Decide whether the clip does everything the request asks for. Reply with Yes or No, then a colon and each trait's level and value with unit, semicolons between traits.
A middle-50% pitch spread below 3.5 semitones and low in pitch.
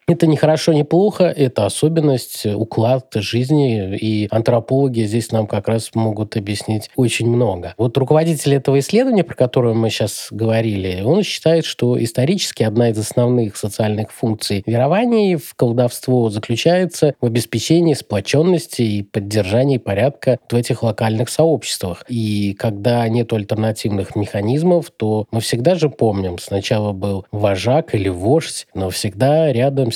No: average, 4.4 semitones; low, 120 Hz